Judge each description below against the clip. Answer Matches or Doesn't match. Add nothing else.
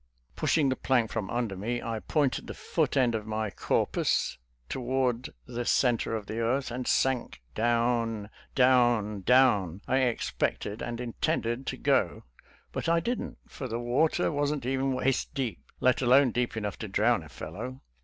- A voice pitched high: Doesn't match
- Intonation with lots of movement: Doesn't match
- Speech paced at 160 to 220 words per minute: Matches